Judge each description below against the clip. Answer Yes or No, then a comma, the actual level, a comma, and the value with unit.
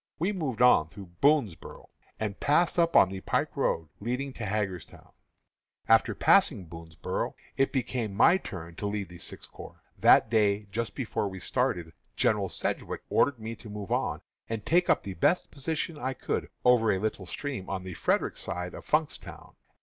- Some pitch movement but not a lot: No, wide, 6.1 semitones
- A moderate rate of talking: Yes, average, 175 wpm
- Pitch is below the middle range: Yes, low, 105 Hz